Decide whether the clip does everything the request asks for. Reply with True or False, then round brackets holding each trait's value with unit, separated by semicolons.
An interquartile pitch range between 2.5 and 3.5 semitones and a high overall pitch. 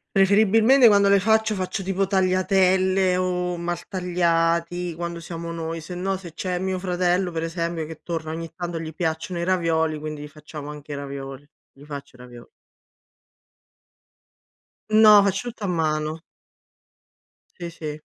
False (2.8 semitones; 175 Hz)